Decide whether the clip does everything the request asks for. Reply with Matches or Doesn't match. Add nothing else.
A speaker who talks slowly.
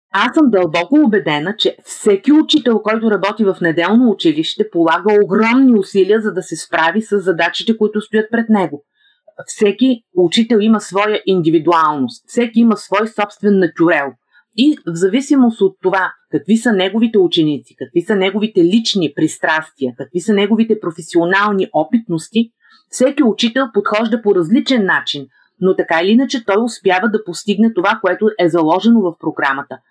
Doesn't match